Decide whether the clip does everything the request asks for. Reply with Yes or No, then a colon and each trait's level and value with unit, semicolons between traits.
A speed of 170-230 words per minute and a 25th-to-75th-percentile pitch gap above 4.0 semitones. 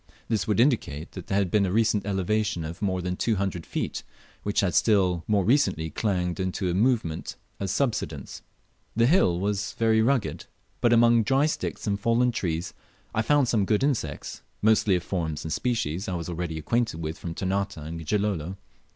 Yes: average, 185 wpm; average, 4.4 semitones